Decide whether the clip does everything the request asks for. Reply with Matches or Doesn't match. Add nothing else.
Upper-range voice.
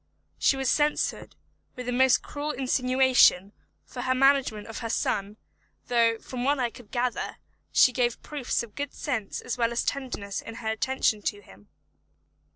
Matches